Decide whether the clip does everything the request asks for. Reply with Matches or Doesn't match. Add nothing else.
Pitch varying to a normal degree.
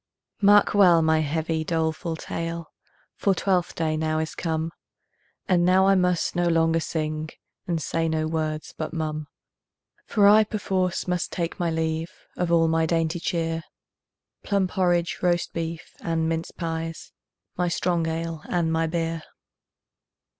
Doesn't match